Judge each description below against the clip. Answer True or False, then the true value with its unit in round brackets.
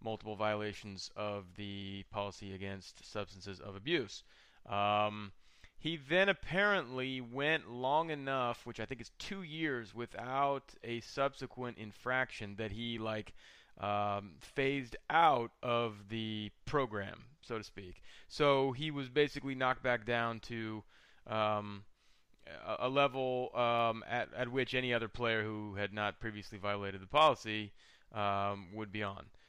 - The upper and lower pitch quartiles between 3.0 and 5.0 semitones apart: True (4.0 semitones)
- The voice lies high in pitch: False (110 Hz)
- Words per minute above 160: False (140 wpm)